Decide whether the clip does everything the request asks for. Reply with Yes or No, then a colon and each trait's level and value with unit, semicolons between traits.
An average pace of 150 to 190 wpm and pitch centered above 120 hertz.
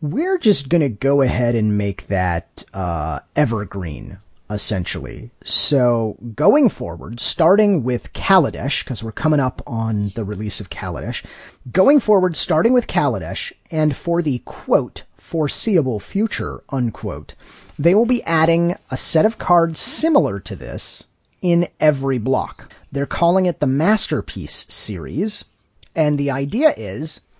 No: slow, 135 wpm; low, 135 Hz